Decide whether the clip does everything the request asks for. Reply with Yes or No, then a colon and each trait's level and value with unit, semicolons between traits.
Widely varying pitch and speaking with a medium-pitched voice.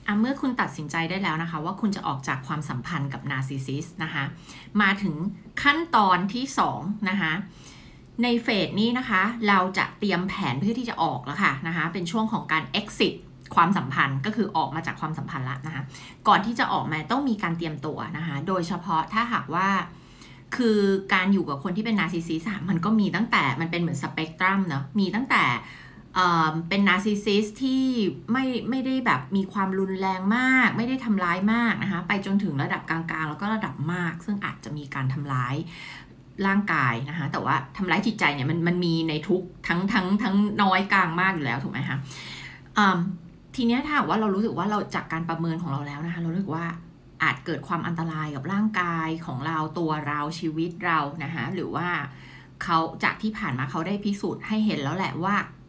No: average, 4.5 semitones; medium, 175 Hz